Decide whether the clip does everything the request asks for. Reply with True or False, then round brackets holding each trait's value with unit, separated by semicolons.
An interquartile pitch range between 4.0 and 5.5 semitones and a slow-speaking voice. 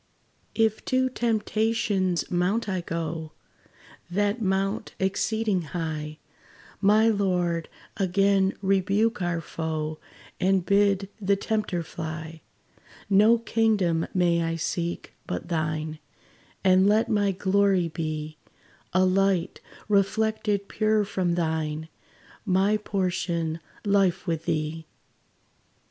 False (3.6 semitones; 100 wpm)